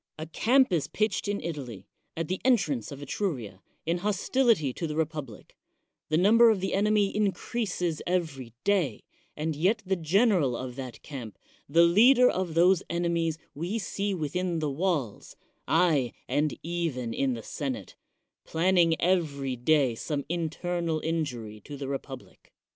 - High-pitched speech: No, medium, 165 Hz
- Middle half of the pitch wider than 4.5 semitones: Yes, average, 5.1 semitones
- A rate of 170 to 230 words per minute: No, average, 155 wpm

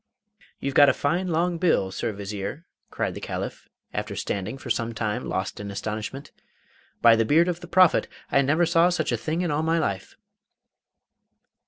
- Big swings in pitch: Yes, wide, 7.5 semitones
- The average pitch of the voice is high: No, medium, 140 Hz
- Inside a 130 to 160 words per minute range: No, average, 180 wpm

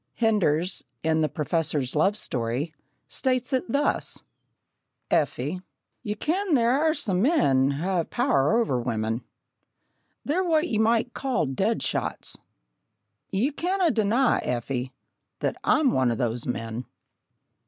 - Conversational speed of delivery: No, slow, 130 wpm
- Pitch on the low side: No, high, 190 Hz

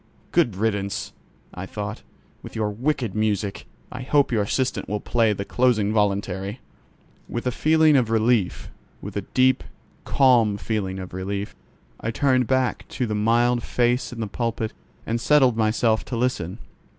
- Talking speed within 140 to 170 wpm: Yes, average, 150 wpm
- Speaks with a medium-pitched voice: No, low, 115 Hz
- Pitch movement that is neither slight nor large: Yes, average, 3.4 semitones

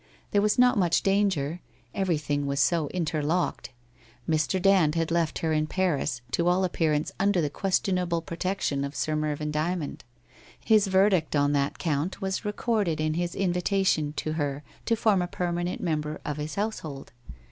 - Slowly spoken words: No, average, 170 wpm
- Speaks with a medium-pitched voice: Yes, medium, 170 Hz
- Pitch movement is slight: No, average, 3.9 semitones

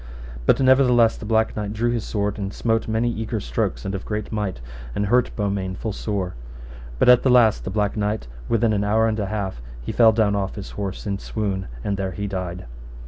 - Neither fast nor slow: No, fast, 215 wpm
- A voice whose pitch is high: No, low, 105 Hz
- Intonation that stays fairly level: Yes, narrow, 2.3 semitones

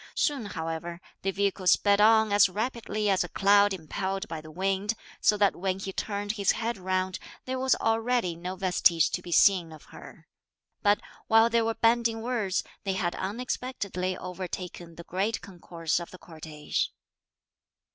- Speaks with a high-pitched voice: Yes, high, 195 Hz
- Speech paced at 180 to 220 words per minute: No, average, 165 wpm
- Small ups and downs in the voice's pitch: No, average, 3.5 semitones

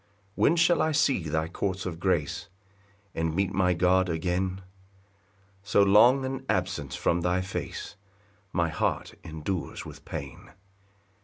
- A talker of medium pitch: No, very low, 95 Hz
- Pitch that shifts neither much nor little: Yes, average, 3.3 semitones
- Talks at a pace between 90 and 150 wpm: Yes, average, 140 wpm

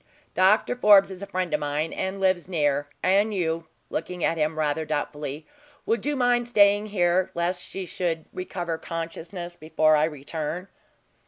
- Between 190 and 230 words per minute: No, average, 160 wpm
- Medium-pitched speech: Yes, medium, 175 Hz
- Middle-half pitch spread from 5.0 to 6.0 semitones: No, average, 3.5 semitones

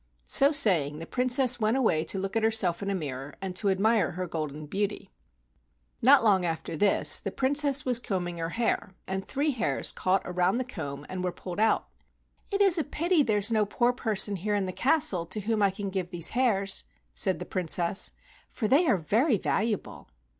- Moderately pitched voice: No, high, 200 Hz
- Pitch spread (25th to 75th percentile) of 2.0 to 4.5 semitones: No, average, 5.3 semitones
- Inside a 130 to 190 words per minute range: No, average, 200 wpm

